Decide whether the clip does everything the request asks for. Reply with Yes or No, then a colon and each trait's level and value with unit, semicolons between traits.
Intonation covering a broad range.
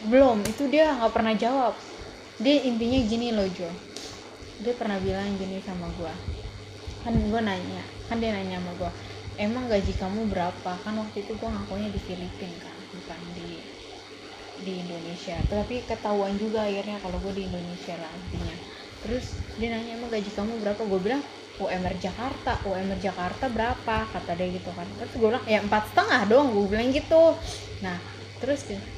No: average, 3.7 semitones